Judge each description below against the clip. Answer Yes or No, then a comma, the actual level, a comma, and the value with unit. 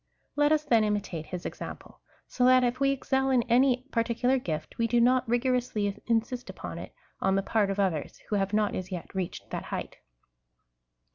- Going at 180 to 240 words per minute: Yes, average, 195 wpm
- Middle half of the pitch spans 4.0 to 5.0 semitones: Yes, average, 4.4 semitones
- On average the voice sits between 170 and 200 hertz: No, high, 230 Hz